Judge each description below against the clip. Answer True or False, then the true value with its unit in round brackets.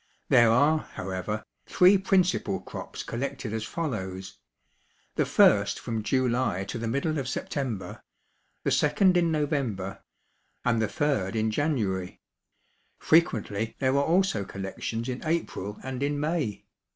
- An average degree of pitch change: False (6.0 semitones)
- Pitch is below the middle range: True (125 Hz)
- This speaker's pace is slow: True (130 wpm)